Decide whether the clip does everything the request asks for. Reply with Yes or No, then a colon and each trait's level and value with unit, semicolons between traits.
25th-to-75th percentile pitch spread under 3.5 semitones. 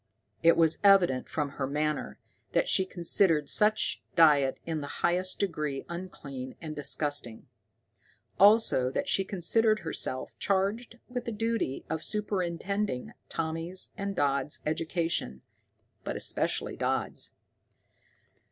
No: average, 5.3 semitones